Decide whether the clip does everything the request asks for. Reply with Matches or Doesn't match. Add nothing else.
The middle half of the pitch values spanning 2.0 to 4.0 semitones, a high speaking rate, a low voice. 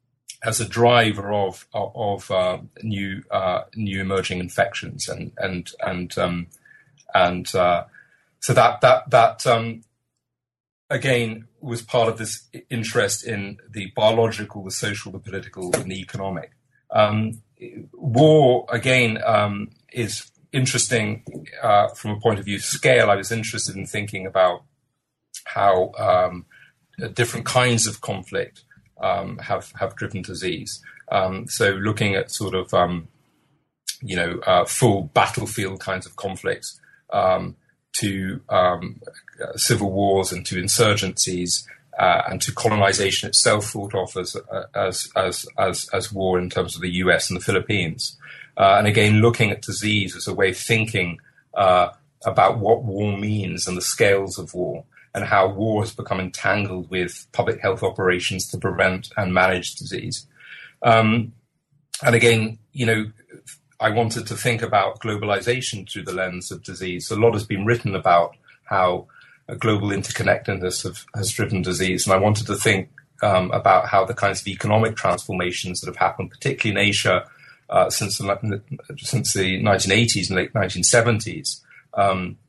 Doesn't match